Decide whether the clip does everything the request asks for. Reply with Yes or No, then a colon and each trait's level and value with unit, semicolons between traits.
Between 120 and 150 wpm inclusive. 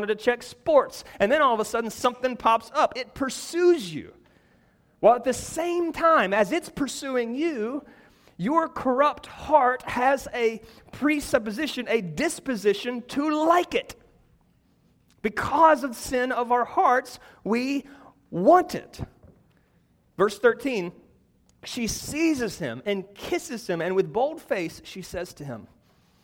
Yes: slow, 135 wpm